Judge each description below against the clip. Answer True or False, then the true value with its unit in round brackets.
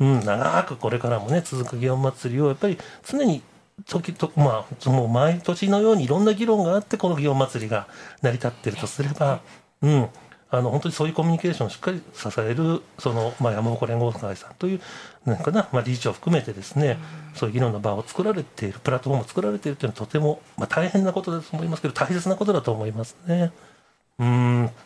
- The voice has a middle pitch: True (145 Hz)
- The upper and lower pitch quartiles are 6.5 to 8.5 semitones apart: False (6.0 semitones)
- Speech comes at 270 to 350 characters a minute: False (455 characters per minute)